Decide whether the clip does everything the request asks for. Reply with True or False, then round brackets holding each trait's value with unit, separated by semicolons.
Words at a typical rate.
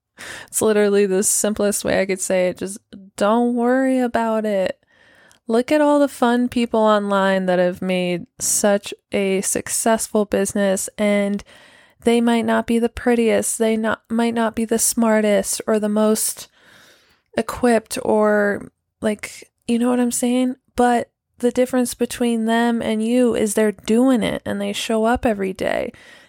True (160 wpm)